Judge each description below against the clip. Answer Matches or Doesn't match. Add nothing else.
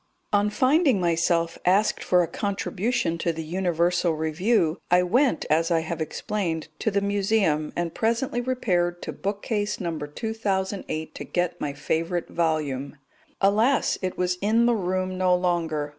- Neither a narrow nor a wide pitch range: Matches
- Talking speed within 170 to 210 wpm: Doesn't match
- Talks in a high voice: Doesn't match